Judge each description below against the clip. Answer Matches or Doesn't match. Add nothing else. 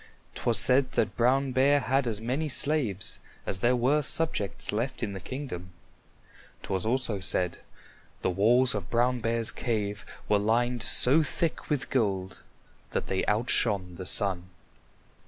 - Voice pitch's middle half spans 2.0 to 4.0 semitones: Doesn't match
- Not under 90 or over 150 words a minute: Matches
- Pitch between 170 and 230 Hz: Doesn't match